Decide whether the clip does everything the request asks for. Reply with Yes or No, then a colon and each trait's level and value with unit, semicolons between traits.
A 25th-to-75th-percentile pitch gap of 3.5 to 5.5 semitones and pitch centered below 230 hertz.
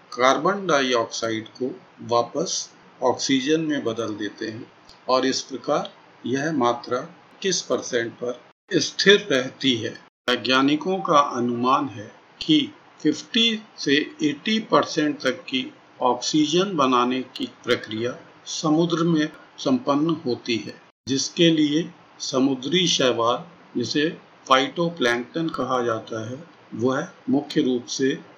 Yes: average, 5.1 semitones; low, 135 Hz